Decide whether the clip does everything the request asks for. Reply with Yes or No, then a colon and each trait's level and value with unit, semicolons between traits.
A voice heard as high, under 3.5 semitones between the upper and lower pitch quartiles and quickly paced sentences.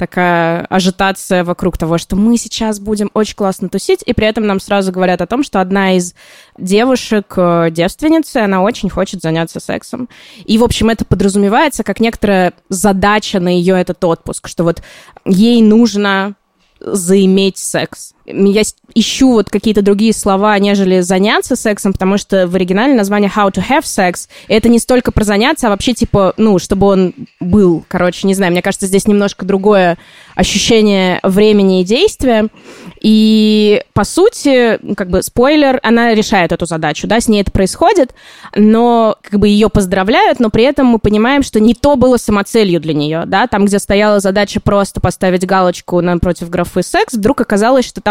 Yes: high, 205 Hz; average, 2.9 semitones; fast, 170 wpm